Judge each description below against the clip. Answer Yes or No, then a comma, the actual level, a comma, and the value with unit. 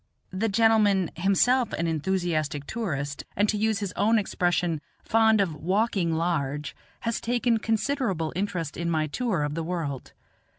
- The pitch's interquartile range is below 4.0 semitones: No, wide, 5.5 semitones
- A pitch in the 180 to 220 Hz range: Yes, medium, 185 Hz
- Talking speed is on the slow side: No, average, 145 wpm